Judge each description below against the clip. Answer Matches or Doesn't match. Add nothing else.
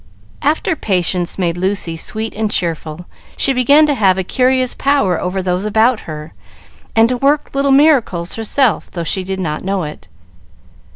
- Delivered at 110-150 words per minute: Doesn't match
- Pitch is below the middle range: Doesn't match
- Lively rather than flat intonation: Matches